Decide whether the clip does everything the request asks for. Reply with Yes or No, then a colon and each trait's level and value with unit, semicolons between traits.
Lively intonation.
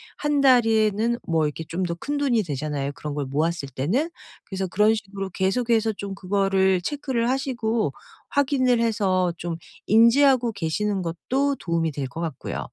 Yes: wide, 6.0 semitones